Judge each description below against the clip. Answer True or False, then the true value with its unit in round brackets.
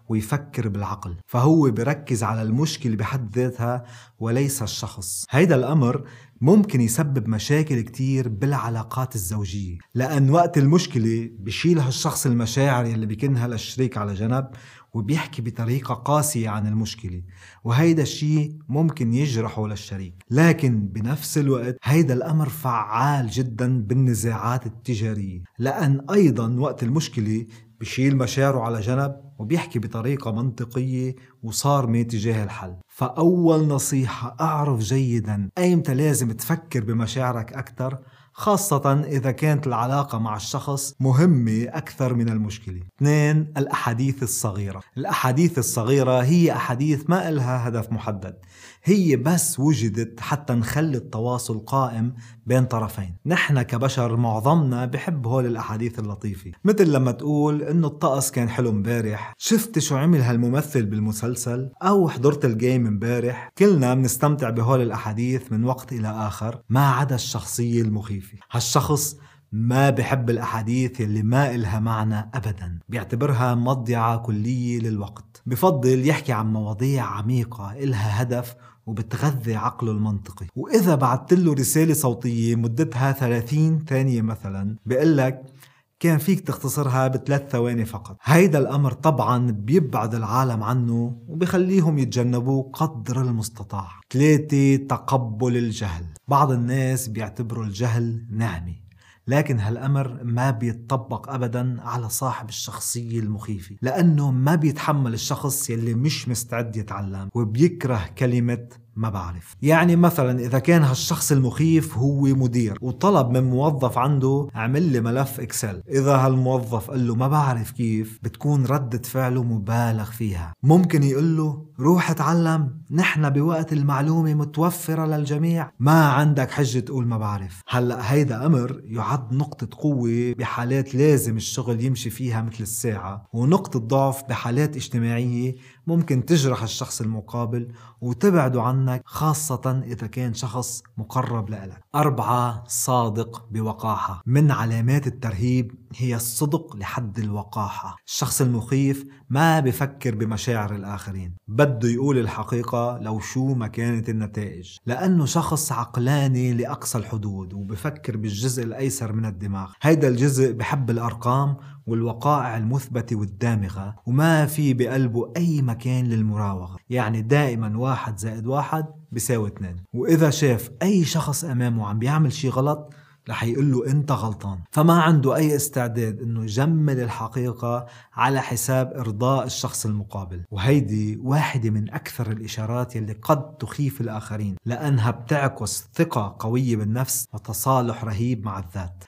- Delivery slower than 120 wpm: False (125 wpm)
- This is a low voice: True (125 Hz)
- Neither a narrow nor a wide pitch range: True (3.7 semitones)